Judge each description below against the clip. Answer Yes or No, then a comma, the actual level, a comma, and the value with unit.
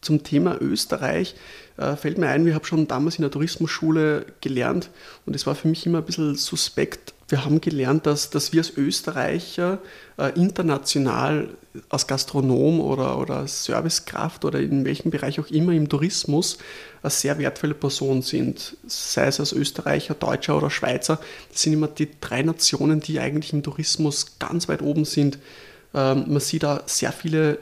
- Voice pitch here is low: No, medium, 150 Hz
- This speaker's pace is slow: No, average, 165 wpm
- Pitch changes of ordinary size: No, narrow, 2.1 semitones